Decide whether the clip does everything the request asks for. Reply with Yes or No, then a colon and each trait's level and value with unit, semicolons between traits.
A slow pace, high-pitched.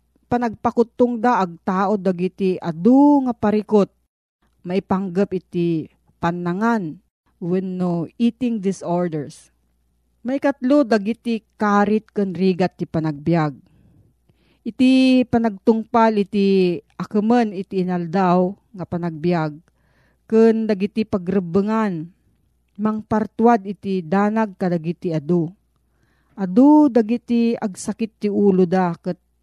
Yes: slow, 95 wpm; high, 200 Hz